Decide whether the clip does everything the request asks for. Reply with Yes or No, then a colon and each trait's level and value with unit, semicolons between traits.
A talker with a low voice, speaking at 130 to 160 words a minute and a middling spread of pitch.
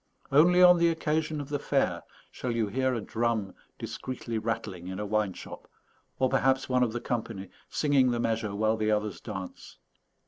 No: low, 115 Hz; average, 180 wpm; average, 3.9 semitones